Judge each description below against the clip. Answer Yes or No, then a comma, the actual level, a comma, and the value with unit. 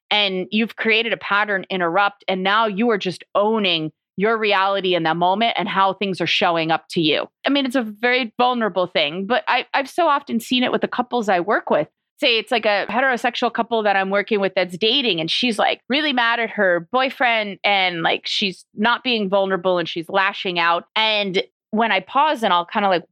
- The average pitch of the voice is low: No, high, 210 Hz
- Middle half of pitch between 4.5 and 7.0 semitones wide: No, average, 3.7 semitones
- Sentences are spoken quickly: Yes, fast, 220 wpm